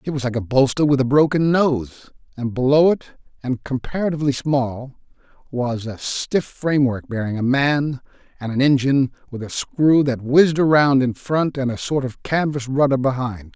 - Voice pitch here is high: No, low, 135 Hz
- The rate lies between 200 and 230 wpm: No, average, 175 wpm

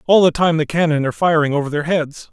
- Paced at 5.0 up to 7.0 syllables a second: Yes, 6.5 syllables/s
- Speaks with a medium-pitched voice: Yes, medium, 160 Hz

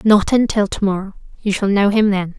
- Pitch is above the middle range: Yes, high, 200 Hz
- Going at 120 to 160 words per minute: No, average, 200 wpm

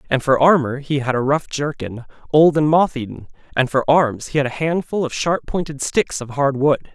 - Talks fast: Yes, fast, 225 wpm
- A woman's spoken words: No, male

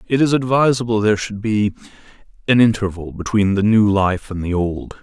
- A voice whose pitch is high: No, low, 105 Hz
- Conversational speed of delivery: Yes, average, 180 wpm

